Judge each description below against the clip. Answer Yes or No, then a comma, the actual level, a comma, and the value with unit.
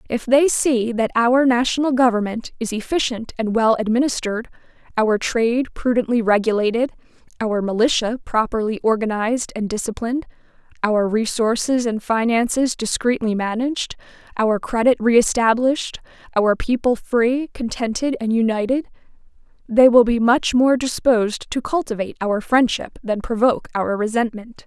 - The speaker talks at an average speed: No, slow, 125 wpm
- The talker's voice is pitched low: No, high, 235 Hz